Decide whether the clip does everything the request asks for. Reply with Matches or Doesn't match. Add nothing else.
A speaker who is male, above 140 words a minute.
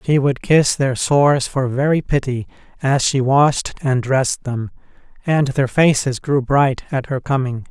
Matches